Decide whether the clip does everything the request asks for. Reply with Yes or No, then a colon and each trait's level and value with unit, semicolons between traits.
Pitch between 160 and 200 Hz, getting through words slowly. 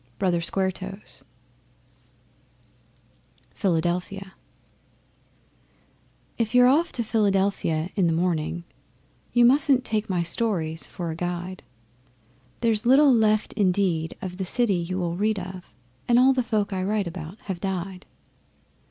Yes: high, 190 Hz; slow, 125 wpm